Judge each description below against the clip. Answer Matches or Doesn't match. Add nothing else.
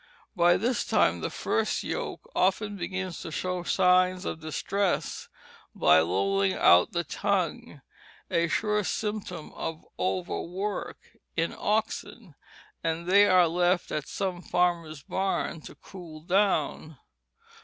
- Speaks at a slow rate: Matches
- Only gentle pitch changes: Doesn't match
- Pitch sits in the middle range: Matches